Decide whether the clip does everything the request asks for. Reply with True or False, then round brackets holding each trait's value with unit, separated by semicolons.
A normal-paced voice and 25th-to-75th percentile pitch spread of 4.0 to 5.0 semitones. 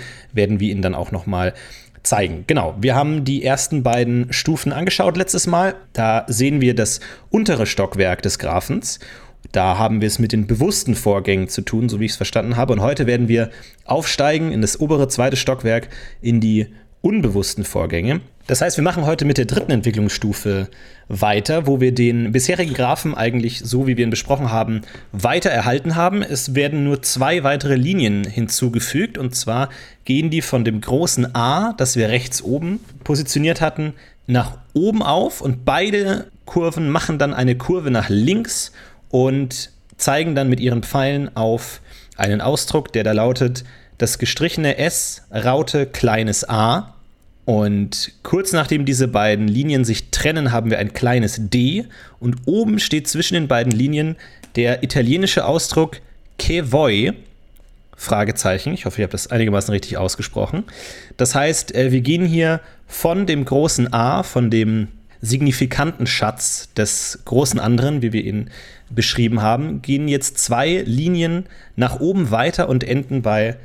True (160 wpm; 4.6 semitones)